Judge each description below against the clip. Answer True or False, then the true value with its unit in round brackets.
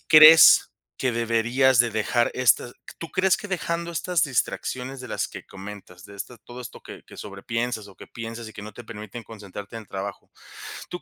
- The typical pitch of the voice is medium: False (115 Hz)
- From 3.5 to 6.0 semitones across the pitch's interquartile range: True (3.9 semitones)